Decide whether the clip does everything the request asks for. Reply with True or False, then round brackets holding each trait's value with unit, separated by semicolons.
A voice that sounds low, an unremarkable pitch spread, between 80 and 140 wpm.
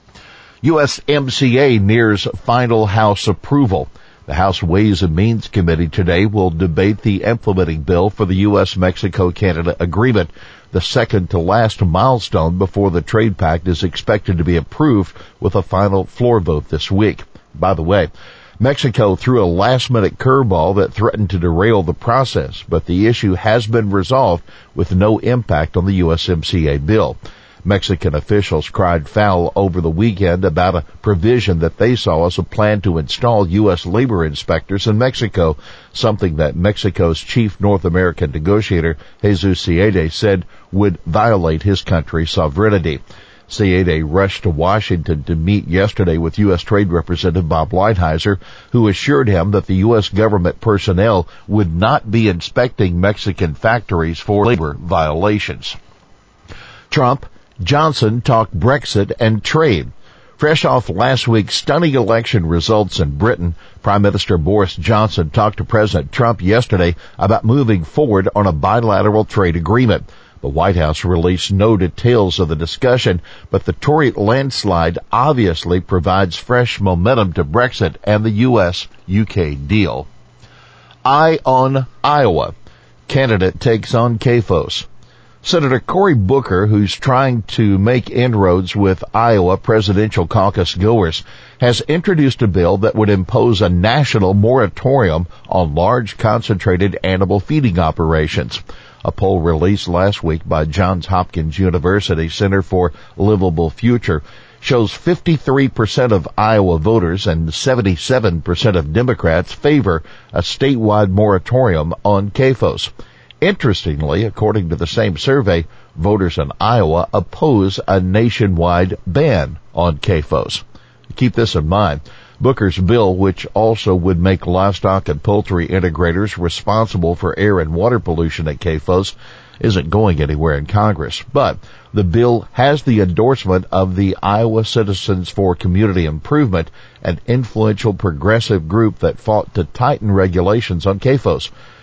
True (100 Hz; 4.1 semitones; 135 wpm)